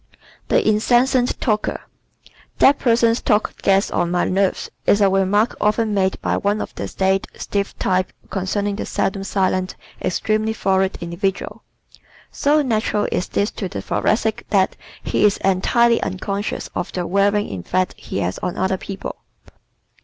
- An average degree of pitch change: No, narrow, 2.3 semitones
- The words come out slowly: No, average, 155 wpm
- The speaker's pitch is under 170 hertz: No, high, 200 Hz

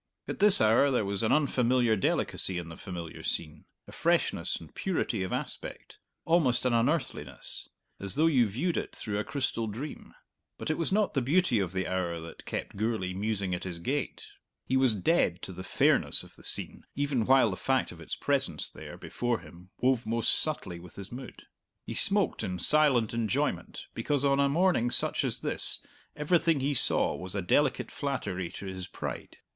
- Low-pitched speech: Yes, low, 115 Hz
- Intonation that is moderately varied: No, wide, 7.1 semitones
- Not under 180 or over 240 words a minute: Yes, average, 190 wpm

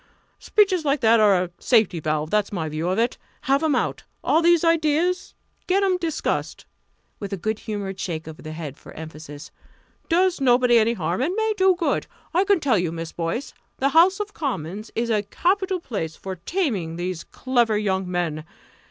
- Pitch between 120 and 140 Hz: No, high, 225 Hz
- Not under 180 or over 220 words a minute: Yes, average, 185 wpm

